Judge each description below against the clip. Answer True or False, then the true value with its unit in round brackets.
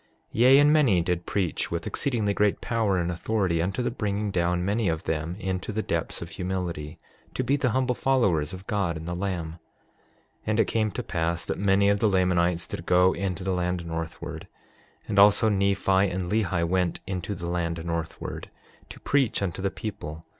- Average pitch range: True (3.4 semitones)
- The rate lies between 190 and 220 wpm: True (195 wpm)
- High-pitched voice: False (95 Hz)